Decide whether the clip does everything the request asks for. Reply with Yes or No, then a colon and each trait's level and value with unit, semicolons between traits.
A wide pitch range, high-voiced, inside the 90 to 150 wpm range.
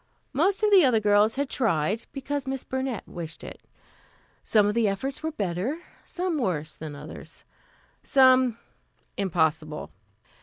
Yes: wide, 7.3 semitones; high, 225 Hz; average, 140 wpm